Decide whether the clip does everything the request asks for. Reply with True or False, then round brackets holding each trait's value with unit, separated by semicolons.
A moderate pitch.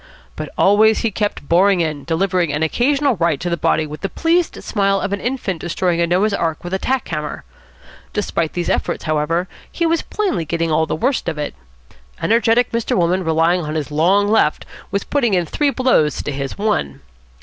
True (180 Hz)